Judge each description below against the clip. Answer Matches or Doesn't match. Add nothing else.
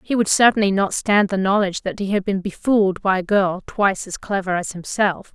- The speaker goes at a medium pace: Doesn't match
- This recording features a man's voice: Doesn't match